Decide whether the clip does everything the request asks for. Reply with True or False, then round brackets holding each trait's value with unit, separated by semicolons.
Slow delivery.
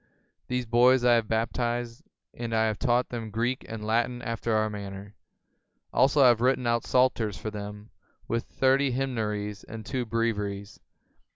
False (160 wpm)